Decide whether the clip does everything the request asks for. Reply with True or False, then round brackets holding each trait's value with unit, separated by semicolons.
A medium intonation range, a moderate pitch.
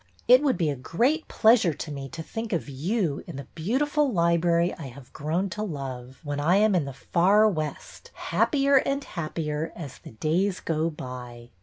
False (6.7 semitones; 170 Hz)